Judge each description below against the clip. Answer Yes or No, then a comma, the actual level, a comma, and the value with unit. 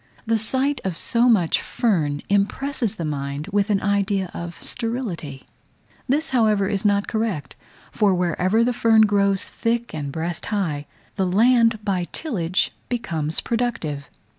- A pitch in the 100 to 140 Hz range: No, high, 200 Hz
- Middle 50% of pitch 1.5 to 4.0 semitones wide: No, average, 5.1 semitones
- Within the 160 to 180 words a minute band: No, average, 140 wpm